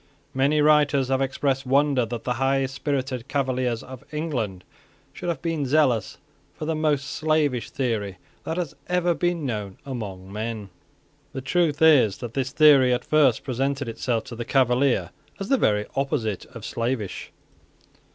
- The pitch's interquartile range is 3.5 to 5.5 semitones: Yes, average, 4.1 semitones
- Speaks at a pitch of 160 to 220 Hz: No, low, 135 Hz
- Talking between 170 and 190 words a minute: No, average, 155 wpm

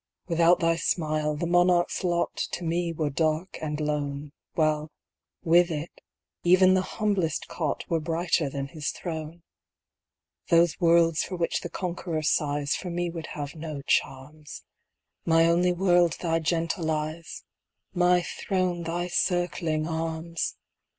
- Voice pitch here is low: No, medium, 165 Hz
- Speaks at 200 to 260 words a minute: No, slow, 135 wpm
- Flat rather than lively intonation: Yes, narrow, 2.1 semitones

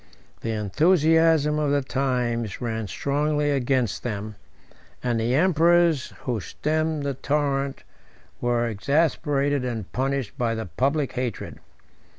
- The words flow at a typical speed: No, slow, 120 wpm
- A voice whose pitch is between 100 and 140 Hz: Yes, low, 135 Hz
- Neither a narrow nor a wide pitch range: Yes, average, 4.1 semitones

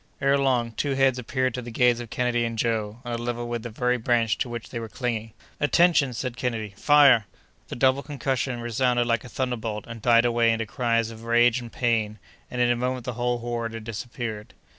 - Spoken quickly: Yes, fast, 215 wpm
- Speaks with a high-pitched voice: No, low, 120 Hz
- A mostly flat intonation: Yes, narrow, 1.6 semitones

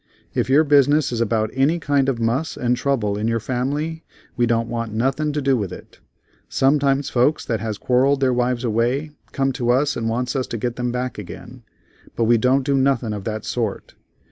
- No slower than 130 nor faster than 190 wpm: No, fast, 205 wpm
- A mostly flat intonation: No, average, 3.0 semitones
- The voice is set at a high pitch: No, low, 125 Hz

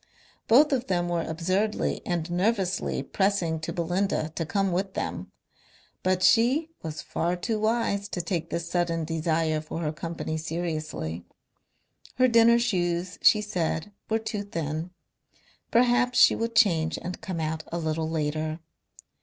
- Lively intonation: No, average, 4.5 semitones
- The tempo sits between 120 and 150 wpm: Yes, average, 145 wpm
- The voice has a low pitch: No, medium, 175 Hz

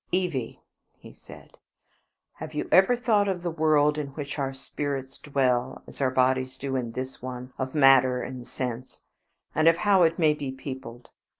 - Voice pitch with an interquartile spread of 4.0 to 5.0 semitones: No, average, 3.3 semitones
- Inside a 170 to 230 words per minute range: Yes, average, 175 wpm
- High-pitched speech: No, low, 135 Hz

